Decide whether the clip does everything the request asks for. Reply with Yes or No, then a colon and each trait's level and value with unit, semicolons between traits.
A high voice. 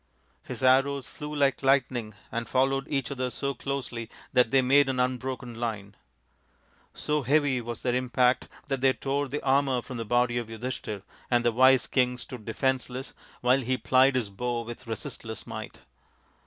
No: low, 130 Hz